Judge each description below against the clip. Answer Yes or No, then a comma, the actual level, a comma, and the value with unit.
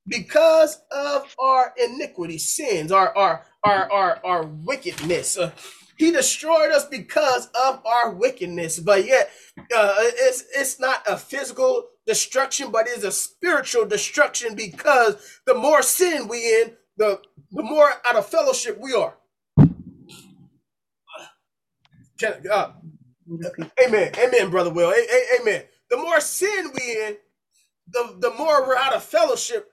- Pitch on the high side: Yes, very high, 265 Hz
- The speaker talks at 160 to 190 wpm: No, slow, 135 wpm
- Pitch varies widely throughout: Yes, wide, 7.4 semitones